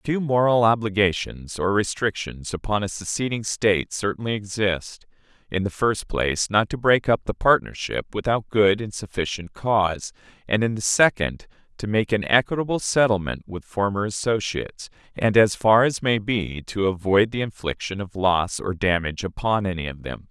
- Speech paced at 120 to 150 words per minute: No, average, 165 wpm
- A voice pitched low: Yes, low, 105 Hz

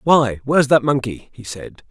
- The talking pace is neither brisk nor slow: Yes, average, 190 wpm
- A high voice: No, low, 130 Hz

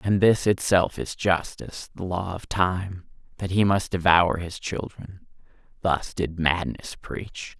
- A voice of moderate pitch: No, very low, 90 Hz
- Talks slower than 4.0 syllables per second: Yes, 3.8 syllables/s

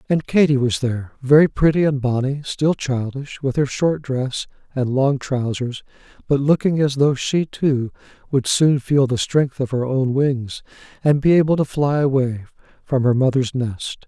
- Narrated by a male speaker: Yes, male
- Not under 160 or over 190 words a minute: Yes, average, 180 wpm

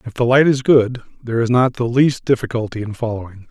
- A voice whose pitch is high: No, low, 120 Hz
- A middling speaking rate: No, fast, 225 wpm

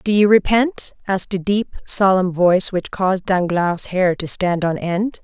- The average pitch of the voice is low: No, high, 190 Hz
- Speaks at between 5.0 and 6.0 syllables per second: No, 4.5 syllables/s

